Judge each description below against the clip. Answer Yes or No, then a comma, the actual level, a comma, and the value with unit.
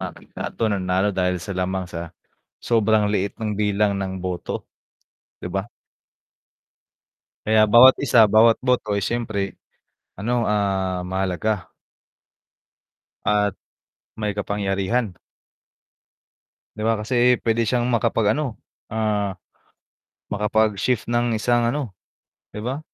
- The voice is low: Yes, low, 105 Hz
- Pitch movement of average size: Yes, average, 3.1 semitones